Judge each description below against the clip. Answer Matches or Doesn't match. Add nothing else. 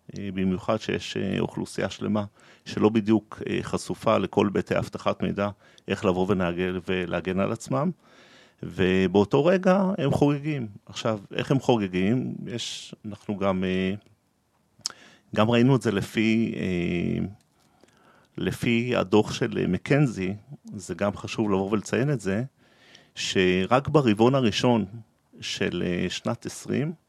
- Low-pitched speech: Matches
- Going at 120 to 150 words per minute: Doesn't match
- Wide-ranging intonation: Doesn't match